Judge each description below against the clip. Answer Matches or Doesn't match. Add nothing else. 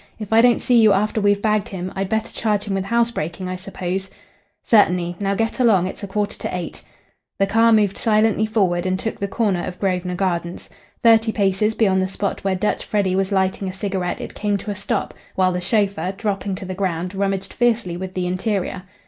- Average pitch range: Doesn't match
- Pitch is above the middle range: Matches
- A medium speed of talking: Doesn't match